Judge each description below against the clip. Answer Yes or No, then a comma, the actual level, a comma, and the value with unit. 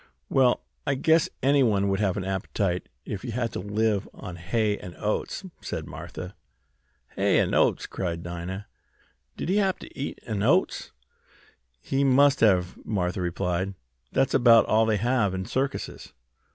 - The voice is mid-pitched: No, low, 105 Hz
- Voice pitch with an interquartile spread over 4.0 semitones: Yes, wide, 5.6 semitones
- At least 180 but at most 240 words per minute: No, average, 160 wpm